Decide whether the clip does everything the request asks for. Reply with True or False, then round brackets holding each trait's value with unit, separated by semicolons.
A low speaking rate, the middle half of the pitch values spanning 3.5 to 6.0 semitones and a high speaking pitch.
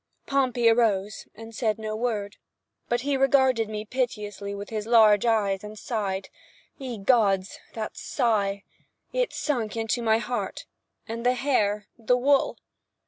False (130 wpm; 2.9 semitones; 225 Hz)